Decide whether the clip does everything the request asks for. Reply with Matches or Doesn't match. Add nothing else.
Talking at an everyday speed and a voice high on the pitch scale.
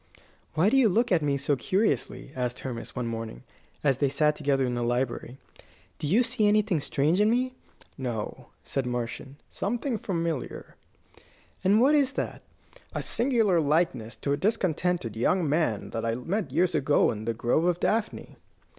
Doesn't match